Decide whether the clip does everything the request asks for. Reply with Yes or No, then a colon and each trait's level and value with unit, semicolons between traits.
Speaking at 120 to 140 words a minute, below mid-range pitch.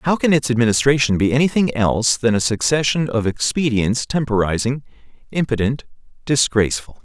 Yes: slow, 135 wpm; low, 125 Hz